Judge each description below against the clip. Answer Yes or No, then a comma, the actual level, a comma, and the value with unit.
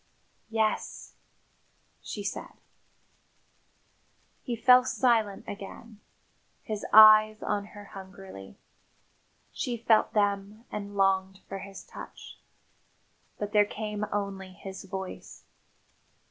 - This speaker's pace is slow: Yes, slow, 95 wpm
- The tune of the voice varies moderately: No, narrow, 1.7 semitones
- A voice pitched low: No, high, 205 Hz